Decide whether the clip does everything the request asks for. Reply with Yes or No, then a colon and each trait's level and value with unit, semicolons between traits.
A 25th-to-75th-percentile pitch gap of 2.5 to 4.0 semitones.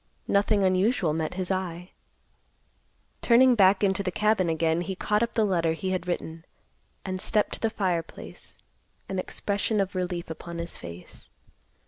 Yes: average, 2.9 semitones